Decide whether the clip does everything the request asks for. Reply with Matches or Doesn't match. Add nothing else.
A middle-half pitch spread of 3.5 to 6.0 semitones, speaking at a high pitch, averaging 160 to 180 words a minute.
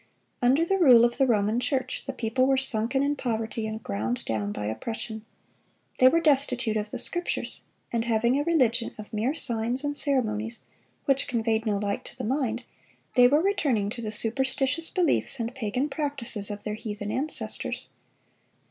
Matches